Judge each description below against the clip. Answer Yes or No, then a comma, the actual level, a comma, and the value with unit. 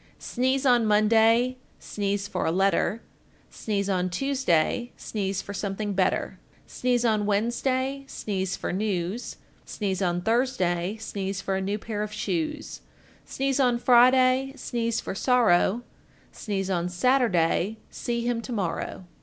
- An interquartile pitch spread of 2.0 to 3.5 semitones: No, average, 4.3 semitones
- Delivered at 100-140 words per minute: Yes, slow, 135 wpm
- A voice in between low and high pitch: No, high, 215 Hz